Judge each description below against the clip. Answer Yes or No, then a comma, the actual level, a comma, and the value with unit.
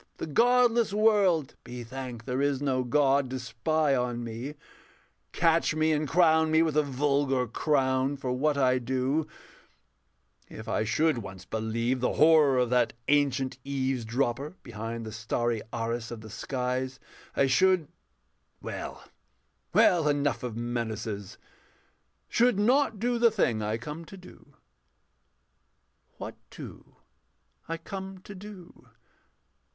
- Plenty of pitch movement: No, average, 4.9 semitones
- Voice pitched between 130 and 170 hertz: Yes, low, 135 Hz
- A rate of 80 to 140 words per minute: Yes, slow, 135 wpm